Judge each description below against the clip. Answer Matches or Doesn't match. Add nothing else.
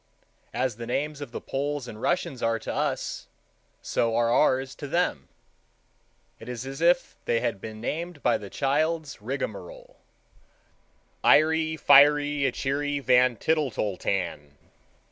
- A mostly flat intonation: Doesn't match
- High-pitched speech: Doesn't match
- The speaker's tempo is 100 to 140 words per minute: Matches